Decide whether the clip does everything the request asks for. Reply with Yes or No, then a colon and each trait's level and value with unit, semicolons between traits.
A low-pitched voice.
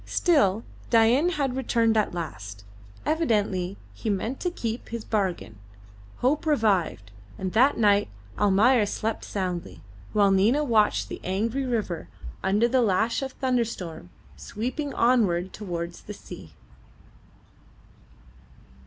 No: high, 215 Hz